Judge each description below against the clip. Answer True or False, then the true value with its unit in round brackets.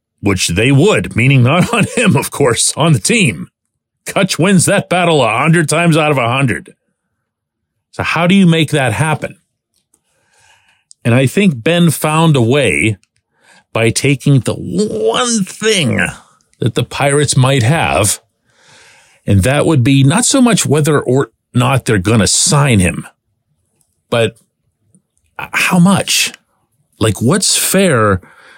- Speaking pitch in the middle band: True (145 Hz)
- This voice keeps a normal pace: True (145 wpm)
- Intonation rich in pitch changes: True (5.7 semitones)